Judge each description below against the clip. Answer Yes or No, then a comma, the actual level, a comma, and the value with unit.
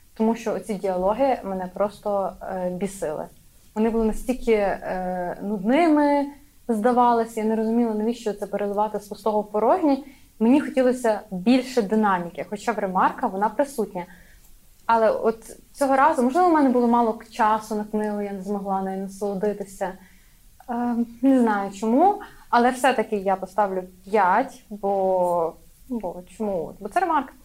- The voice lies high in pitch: Yes, high, 215 Hz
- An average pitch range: Yes, average, 3.7 semitones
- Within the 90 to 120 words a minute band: No, average, 140 wpm